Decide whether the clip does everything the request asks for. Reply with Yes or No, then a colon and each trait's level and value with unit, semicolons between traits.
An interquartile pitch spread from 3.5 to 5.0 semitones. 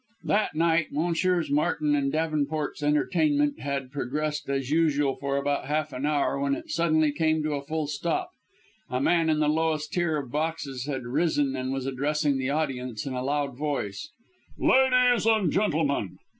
No: narrow, 2.4 semitones